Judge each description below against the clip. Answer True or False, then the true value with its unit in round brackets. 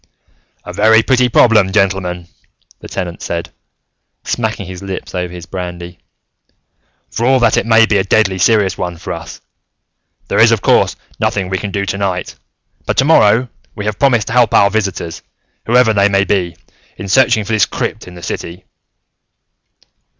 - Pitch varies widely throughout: False (3.6 semitones)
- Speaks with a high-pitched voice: False (100 Hz)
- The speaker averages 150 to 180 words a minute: True (165 wpm)